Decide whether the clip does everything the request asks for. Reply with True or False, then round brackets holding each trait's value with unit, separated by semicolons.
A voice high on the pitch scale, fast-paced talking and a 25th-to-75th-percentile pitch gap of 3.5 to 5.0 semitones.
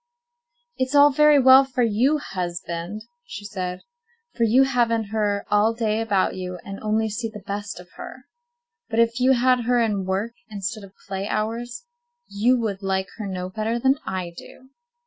False (215 Hz; 180 wpm; 3.8 semitones)